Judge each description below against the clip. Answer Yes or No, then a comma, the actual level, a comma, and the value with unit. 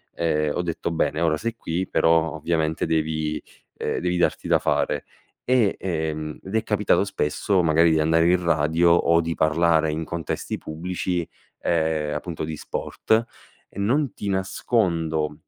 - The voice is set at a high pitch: No, very low, 85 Hz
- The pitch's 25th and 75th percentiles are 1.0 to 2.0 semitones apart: No, narrow, 2.5 semitones